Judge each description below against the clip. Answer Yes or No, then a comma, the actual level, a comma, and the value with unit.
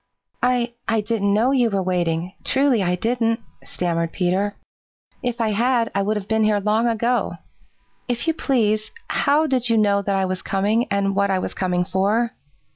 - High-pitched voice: Yes, high, 215 Hz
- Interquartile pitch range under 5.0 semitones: Yes, average, 3.4 semitones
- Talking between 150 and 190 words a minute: Yes, average, 185 wpm